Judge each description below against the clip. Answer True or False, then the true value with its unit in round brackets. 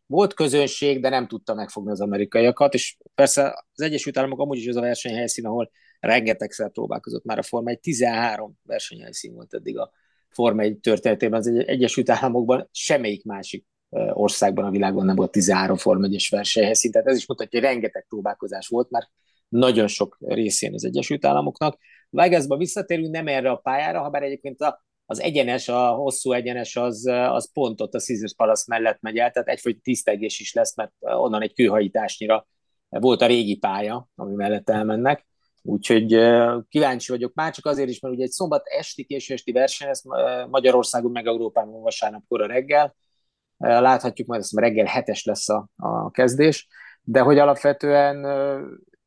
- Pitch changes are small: False (3.5 semitones)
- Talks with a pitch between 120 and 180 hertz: True (125 Hz)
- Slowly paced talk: False (170 wpm)